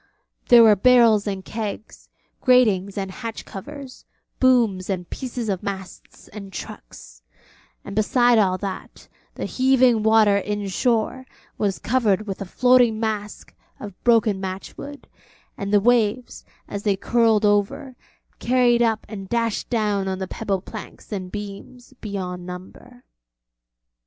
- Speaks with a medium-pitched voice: No, high, 215 Hz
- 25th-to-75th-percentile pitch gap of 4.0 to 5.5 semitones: No, average, 3.5 semitones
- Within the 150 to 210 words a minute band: No, slow, 135 wpm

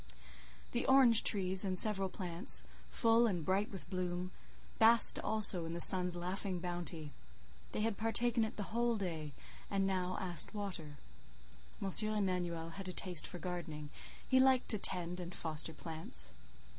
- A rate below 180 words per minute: Yes, average, 155 wpm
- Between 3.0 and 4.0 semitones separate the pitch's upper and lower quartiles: Yes, average, 3.5 semitones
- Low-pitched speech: No, medium, 185 Hz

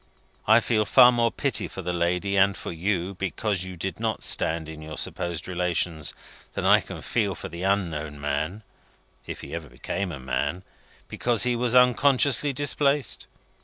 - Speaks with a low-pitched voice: Yes, very low, 95 Hz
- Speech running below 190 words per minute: Yes, average, 170 wpm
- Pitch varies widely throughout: Yes, wide, 5.7 semitones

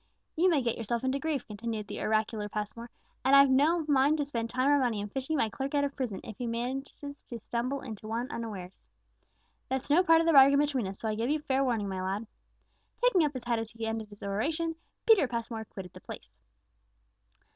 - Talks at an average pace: No, fast, 220 wpm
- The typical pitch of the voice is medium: No, high, 245 Hz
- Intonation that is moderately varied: Yes, average, 4.3 semitones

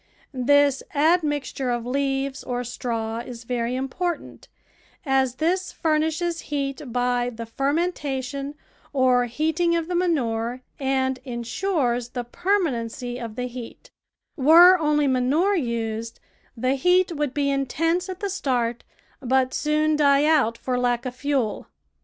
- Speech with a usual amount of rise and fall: Yes, average, 4.0 semitones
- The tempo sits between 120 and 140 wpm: Yes, slow, 135 wpm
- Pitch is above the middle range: Yes, very high, 270 Hz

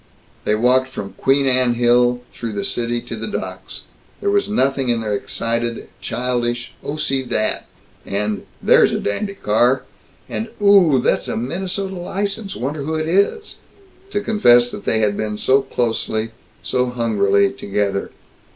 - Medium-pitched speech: No, low, 125 Hz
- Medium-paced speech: Yes, average, 155 wpm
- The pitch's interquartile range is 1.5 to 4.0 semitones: No, wide, 5.5 semitones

